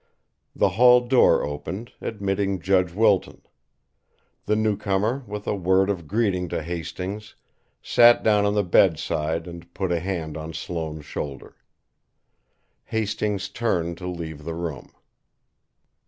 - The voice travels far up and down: No, average, 3.9 semitones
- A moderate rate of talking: No, slow, 125 wpm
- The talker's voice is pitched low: Yes, very low, 95 Hz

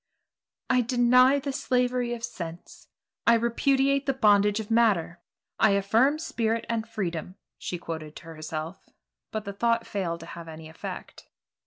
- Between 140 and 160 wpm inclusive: Yes, average, 150 wpm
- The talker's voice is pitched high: Yes, high, 220 Hz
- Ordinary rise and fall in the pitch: No, wide, 6.2 semitones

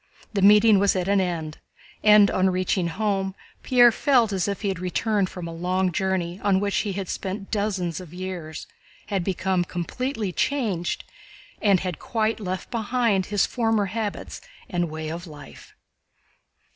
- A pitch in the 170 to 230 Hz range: Yes, high, 190 Hz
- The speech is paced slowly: No, average, 160 wpm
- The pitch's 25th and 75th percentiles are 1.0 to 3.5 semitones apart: Yes, average, 2.8 semitones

